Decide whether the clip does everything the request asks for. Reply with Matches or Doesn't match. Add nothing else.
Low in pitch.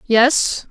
Doesn't match